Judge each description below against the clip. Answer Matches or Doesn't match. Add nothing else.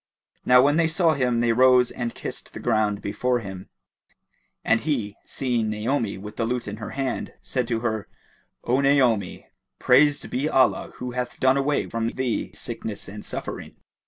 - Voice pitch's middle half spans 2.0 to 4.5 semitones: Matches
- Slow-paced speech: Doesn't match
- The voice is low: Matches